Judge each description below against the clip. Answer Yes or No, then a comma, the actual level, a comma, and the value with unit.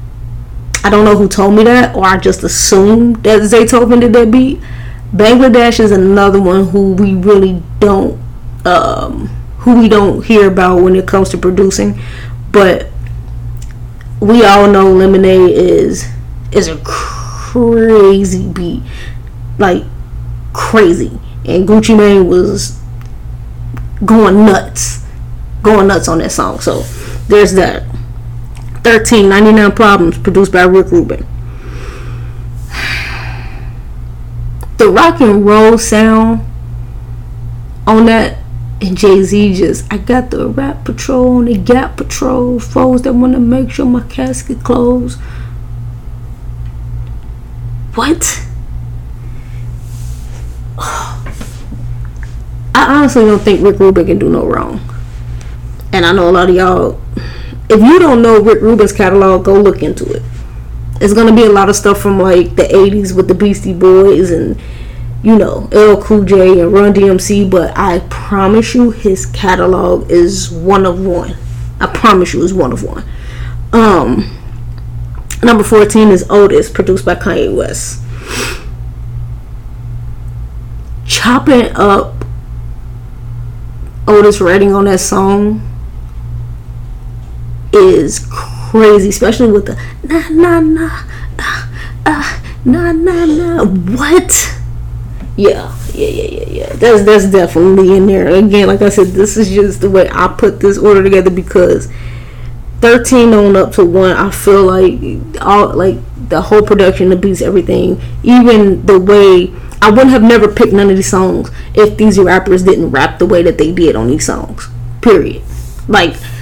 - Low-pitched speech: No, medium, 185 Hz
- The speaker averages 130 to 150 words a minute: Yes, slow, 135 wpm